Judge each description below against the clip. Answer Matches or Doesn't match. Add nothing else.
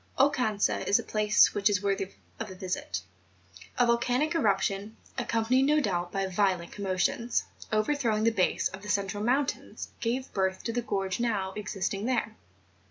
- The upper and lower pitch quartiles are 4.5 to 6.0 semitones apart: Doesn't match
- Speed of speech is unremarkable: Matches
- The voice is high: Matches